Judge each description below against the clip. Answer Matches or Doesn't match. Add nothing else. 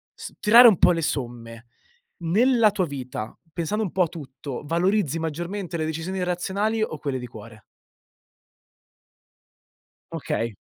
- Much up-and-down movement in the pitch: Matches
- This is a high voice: Doesn't match